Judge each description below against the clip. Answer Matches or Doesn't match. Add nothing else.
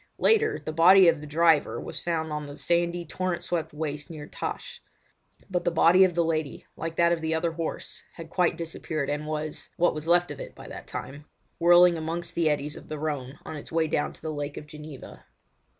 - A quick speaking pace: Matches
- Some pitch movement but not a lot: Doesn't match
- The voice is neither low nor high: Matches